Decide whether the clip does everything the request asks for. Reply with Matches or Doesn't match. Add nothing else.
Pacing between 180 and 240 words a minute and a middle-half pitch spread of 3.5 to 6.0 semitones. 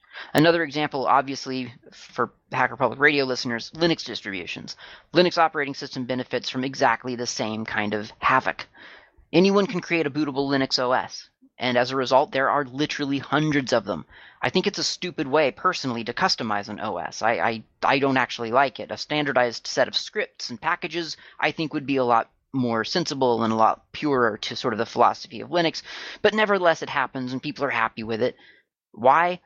Matches